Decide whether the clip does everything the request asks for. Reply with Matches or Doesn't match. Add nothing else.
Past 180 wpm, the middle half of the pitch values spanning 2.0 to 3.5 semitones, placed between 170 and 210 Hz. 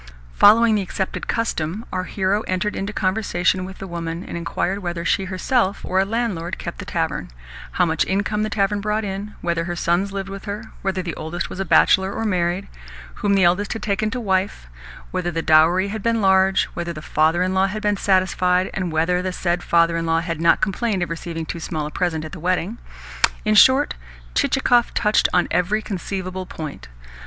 Matches